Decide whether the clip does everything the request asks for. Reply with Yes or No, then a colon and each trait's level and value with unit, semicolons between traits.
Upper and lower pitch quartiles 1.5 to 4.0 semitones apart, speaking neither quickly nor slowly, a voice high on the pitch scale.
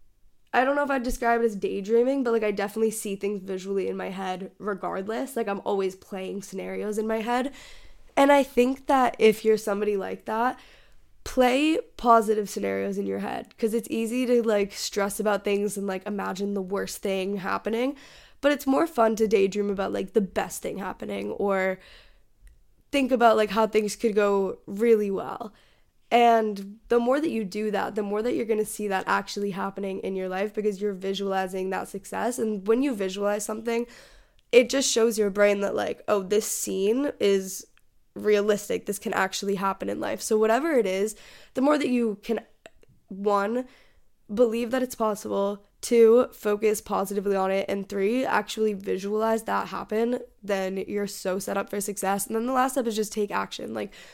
Yes: average, 2.7 semitones; average, 190 wpm; high, 210 Hz